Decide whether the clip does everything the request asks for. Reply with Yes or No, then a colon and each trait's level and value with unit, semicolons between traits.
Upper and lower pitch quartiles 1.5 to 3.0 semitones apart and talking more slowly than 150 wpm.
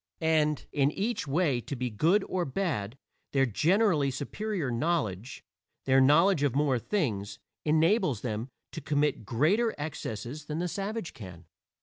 No: wide, 5.5 semitones; average, 140 wpm